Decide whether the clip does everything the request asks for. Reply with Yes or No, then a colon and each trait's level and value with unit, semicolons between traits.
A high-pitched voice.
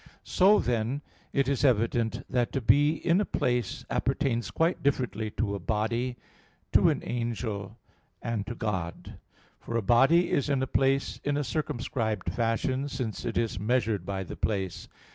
No: low, 120 Hz